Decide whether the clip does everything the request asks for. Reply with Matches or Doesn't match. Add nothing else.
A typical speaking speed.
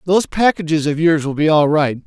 Doesn't match